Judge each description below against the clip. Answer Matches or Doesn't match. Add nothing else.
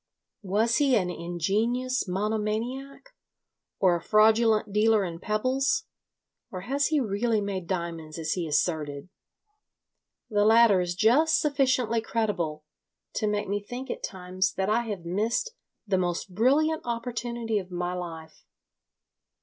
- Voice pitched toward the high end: Matches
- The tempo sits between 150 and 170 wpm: Doesn't match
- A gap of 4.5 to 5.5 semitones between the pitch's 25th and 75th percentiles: Matches